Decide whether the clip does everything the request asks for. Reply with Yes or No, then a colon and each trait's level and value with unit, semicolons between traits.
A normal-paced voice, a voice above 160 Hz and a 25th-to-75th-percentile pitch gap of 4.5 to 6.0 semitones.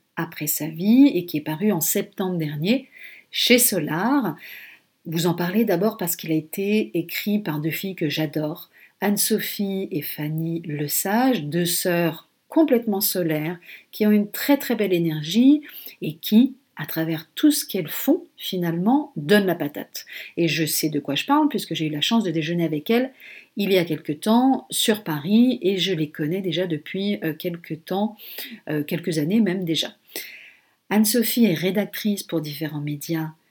Yes: average, 170 wpm; medium, 185 Hz; average, 5.2 semitones